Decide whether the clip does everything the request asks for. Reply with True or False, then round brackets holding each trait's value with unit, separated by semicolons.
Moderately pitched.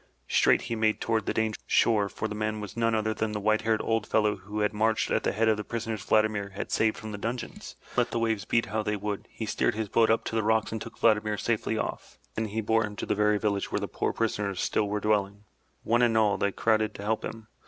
False (110 Hz)